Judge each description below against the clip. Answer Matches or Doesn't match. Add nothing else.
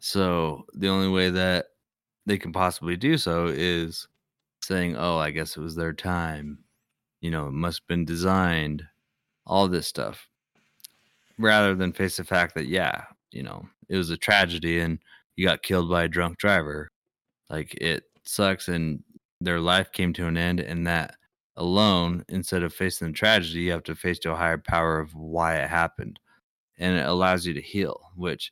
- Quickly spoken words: Doesn't match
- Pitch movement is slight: Matches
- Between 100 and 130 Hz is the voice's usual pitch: Doesn't match